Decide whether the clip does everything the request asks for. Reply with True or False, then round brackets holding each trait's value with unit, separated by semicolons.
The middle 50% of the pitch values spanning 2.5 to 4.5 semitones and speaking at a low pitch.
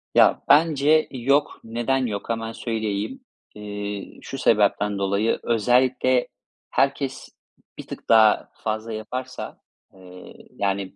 True (4.0 semitones; 115 Hz)